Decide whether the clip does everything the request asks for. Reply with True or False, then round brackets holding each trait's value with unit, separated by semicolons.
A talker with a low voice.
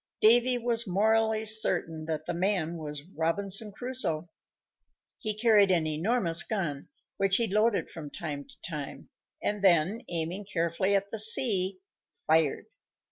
False (190 Hz)